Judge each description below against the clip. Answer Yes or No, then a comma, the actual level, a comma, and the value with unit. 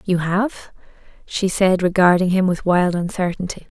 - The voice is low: No, medium, 185 Hz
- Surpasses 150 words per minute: No, average, 140 wpm